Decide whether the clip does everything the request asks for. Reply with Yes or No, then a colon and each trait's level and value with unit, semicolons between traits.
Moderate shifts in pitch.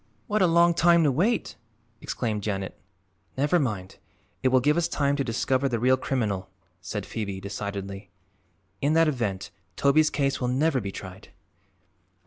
No: wide, 6.9 semitones